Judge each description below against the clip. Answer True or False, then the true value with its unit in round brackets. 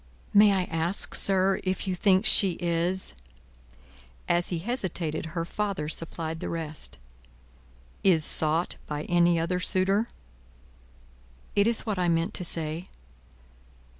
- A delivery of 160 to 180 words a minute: False (135 wpm)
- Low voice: False (175 Hz)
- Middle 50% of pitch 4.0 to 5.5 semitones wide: False (2.7 semitones)